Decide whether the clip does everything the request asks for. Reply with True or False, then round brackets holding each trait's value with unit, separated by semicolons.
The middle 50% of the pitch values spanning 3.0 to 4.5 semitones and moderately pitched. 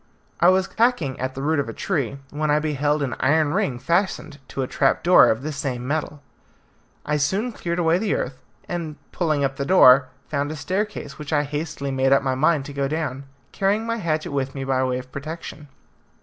True (3.5 semitones; 145 Hz)